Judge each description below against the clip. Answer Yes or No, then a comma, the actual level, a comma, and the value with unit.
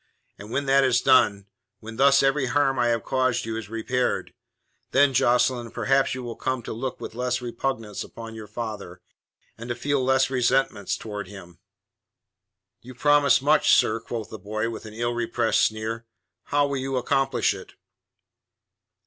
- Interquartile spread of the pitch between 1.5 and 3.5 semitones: Yes, average, 3.1 semitones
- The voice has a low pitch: Yes, low, 120 Hz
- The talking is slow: No, average, 165 wpm